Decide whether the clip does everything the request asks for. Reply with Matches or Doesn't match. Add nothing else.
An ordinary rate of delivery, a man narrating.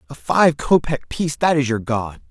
Matches